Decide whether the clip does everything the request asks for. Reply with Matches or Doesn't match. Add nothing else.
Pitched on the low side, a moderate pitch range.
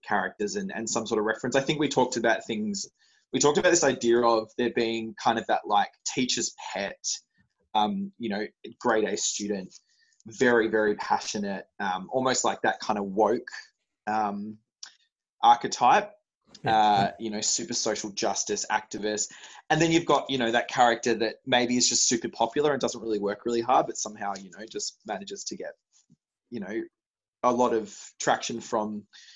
Doesn't match